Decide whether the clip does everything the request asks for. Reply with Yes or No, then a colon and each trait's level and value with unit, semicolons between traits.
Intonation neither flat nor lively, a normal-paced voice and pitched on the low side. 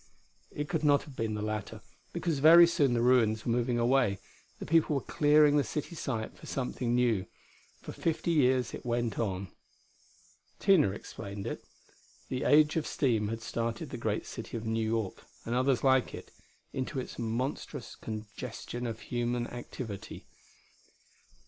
Yes: average, 4.0 semitones; average, 160 wpm; low, 120 Hz